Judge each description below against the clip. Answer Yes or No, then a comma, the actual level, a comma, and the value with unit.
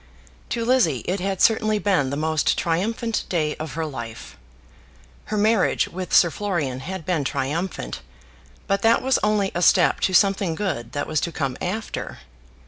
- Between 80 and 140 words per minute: No, average, 165 wpm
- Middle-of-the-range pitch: Yes, medium, 180 Hz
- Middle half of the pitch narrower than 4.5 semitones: No, average, 5.2 semitones